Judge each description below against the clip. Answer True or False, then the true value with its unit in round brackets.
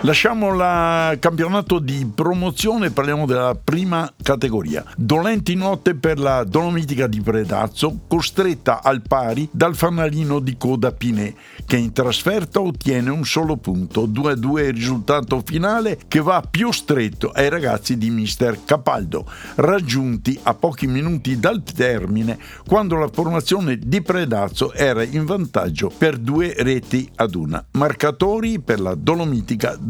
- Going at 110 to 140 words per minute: True (135 wpm)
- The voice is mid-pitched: True (145 Hz)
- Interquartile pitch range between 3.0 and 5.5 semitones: True (5.2 semitones)